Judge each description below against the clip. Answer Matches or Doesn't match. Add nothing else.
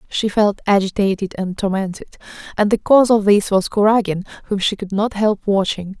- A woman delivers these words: Matches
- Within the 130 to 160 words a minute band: Doesn't match